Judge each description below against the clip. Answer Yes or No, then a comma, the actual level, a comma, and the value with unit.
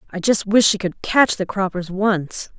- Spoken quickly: Yes, fast, 210 wpm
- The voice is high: Yes, high, 195 Hz